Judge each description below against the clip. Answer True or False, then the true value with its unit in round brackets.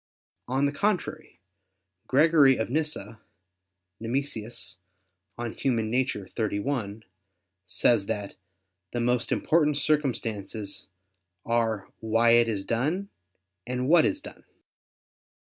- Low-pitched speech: True (120 Hz)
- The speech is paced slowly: True (100 wpm)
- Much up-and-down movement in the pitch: False (4.4 semitones)